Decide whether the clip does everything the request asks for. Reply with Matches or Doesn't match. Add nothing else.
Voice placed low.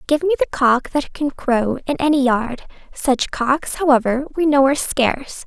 Doesn't match